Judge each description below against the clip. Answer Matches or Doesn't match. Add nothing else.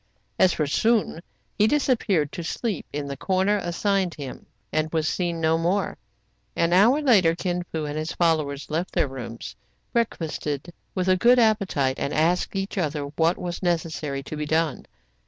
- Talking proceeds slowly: Doesn't match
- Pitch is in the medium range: Matches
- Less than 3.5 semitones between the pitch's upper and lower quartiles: Doesn't match